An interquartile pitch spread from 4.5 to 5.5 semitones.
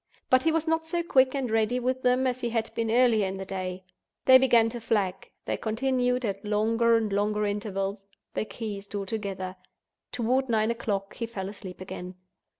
No: average, 3.9 semitones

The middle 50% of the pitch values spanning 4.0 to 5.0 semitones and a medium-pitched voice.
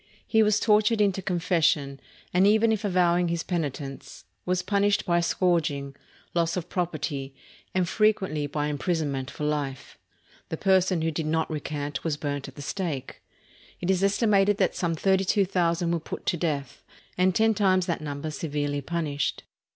Yes: average, 4.4 semitones; medium, 170 Hz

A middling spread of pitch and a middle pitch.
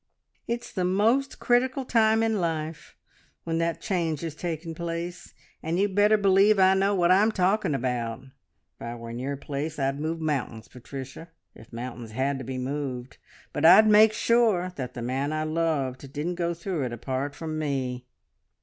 No: wide, 6.2 semitones; medium, 160 Hz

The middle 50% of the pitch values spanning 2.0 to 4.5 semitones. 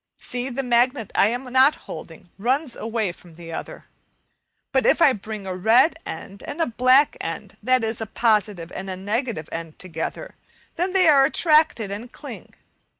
No: average, 5.3 semitones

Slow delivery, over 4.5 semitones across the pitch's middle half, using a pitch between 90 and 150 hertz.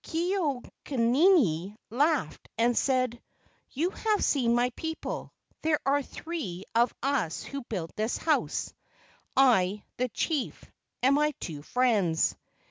No: slow, 125 wpm; wide, 5.4 semitones; very high, 255 Hz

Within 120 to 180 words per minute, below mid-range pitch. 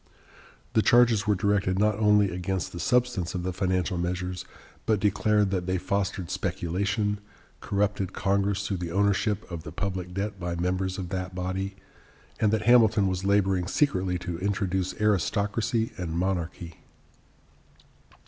Yes: average, 145 wpm; very low, 95 Hz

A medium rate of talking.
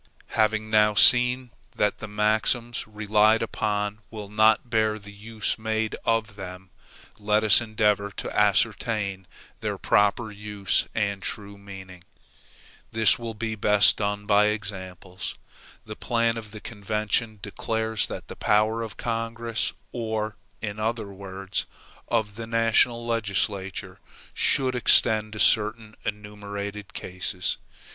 No: slow, 125 wpm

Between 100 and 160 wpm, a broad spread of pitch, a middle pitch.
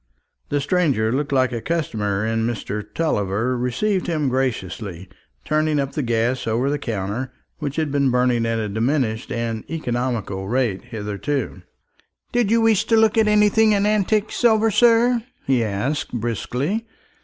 No: average, 155 wpm; wide, 7.4 semitones; low, 130 Hz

